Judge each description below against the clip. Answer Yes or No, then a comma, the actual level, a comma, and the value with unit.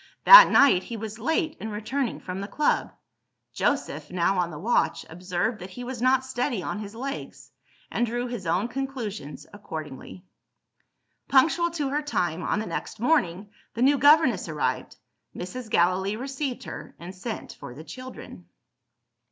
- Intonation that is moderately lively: No, wide, 6.4 semitones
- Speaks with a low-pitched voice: No, high, 225 Hz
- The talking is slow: No, average, 160 wpm